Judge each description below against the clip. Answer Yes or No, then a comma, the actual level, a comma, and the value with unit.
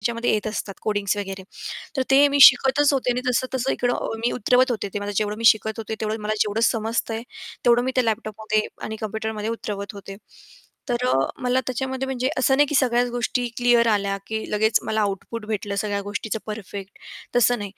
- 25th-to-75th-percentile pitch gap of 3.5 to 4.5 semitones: No, average, 2.8 semitones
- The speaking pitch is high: Yes, high, 225 Hz